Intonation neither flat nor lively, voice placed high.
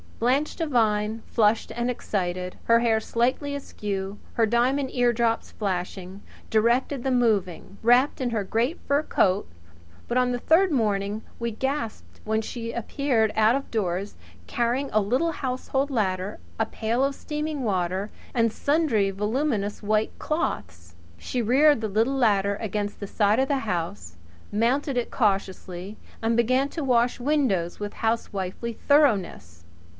Yes: average, 4.2 semitones; high, 230 Hz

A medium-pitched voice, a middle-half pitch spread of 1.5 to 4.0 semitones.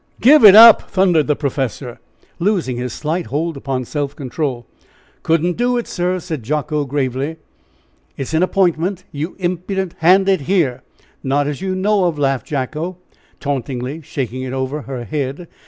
No: medium, 150 Hz; average, 5.2 semitones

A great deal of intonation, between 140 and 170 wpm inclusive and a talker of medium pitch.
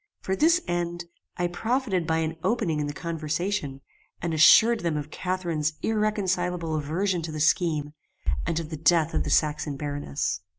No: average, 3.4 semitones; average, 165 wpm; medium, 165 Hz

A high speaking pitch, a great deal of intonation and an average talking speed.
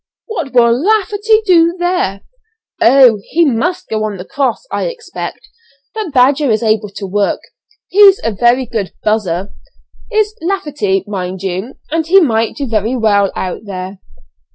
Yes: high, 240 Hz; wide, 8.9 semitones; average, 155 wpm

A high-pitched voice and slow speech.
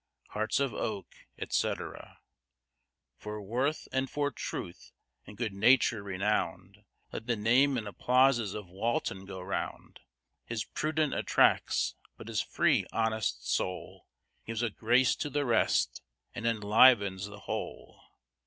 No: low, 110 Hz; slow, 130 wpm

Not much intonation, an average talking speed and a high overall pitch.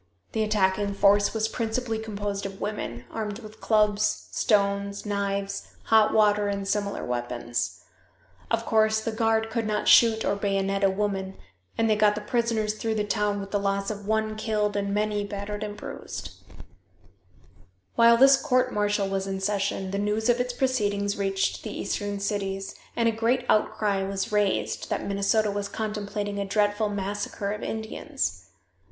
Yes: narrow, 1.5 semitones; average, 165 wpm; high, 205 Hz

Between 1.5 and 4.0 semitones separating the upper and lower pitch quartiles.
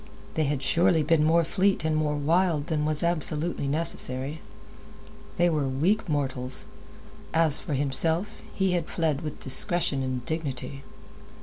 Yes: average, 3.2 semitones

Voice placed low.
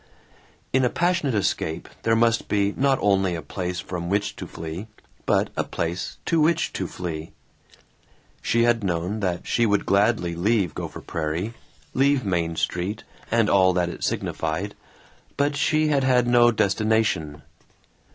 Yes: low, 100 Hz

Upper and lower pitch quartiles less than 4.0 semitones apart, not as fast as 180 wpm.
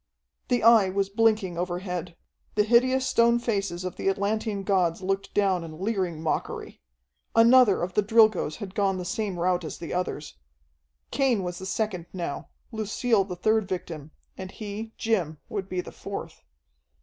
Yes: average, 3.5 semitones; average, 160 wpm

